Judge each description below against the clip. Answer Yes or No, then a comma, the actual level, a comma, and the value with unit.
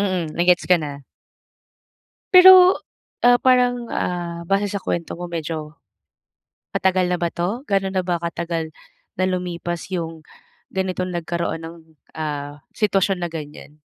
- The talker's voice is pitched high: No, medium, 175 Hz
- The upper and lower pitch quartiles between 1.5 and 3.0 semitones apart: Yes, average, 2.7 semitones